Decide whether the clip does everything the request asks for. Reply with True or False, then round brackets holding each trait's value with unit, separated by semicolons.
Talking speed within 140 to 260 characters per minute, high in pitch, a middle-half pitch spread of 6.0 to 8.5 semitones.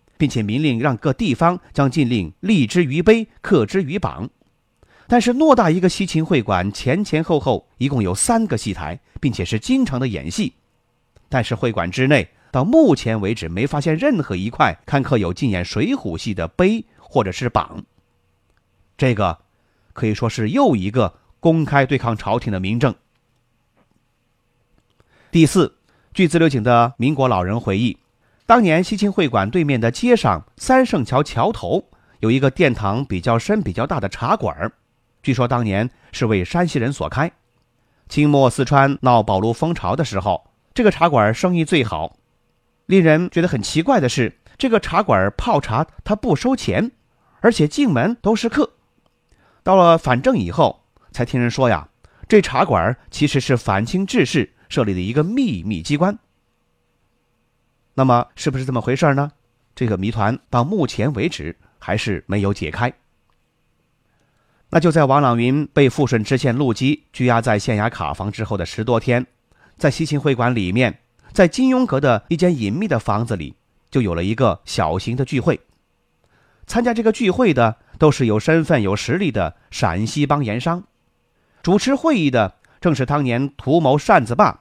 False (245 characters per minute; 125 Hz; 6.3 semitones)